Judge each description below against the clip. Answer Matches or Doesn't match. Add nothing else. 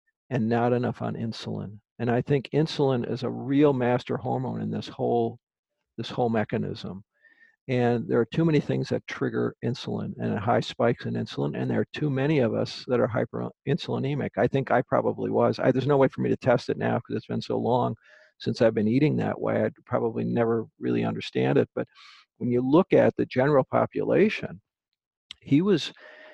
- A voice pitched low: Matches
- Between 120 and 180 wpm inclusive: Doesn't match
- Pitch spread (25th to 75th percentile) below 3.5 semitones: Doesn't match